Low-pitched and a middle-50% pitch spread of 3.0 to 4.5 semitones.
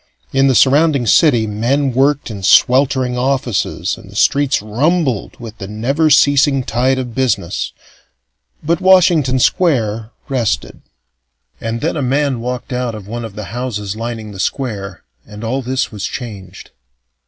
Yes: low, 125 Hz; average, 4.0 semitones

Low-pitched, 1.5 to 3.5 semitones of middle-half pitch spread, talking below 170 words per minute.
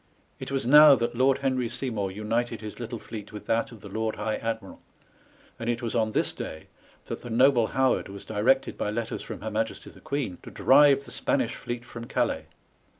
No: low, 115 Hz; average, 3.0 semitones; fast, 205 wpm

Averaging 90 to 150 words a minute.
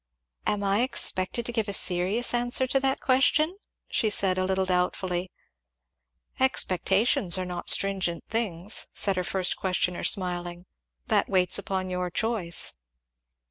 Yes: average, 140 wpm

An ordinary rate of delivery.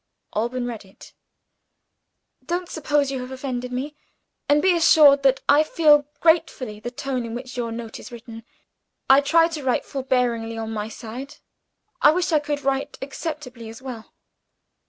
Yes: average, 160 wpm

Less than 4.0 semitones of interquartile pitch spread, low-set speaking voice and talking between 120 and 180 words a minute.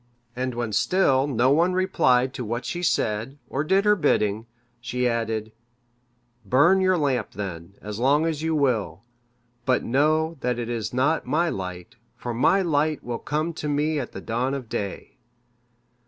No: average, 5.1 semitones; low, 130 Hz; average, 170 wpm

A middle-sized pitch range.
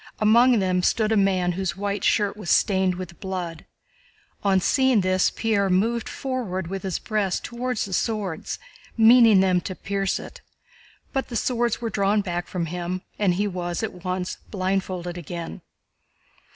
Yes: average, 3.0 semitones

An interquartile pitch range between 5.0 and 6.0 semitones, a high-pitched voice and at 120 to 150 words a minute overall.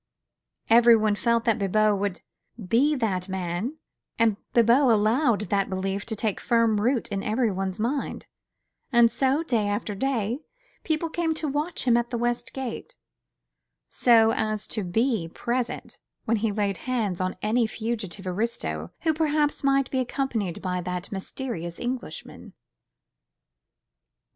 No: average, 4.1 semitones; high, 225 Hz; average, 140 wpm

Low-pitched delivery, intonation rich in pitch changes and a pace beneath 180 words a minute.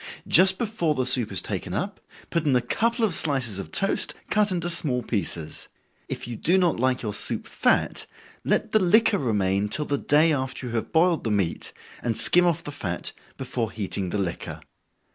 No: low, 130 Hz; wide, 8.1 semitones; average, 195 wpm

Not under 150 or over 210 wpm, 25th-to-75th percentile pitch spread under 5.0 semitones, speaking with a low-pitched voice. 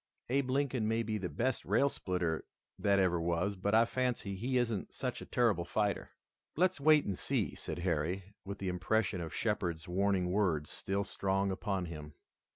Yes: average, 175 wpm; average, 4.2 semitones; low, 100 Hz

